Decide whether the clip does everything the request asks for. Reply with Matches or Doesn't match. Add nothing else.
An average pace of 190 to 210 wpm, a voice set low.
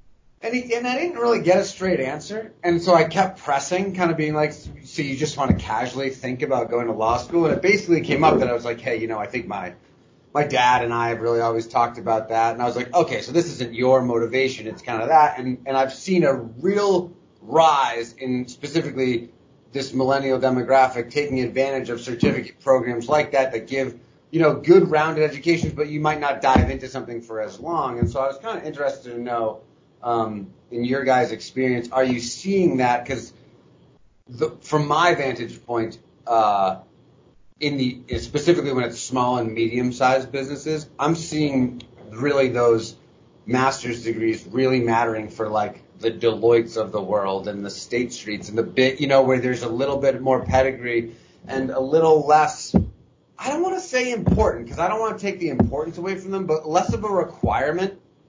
Matches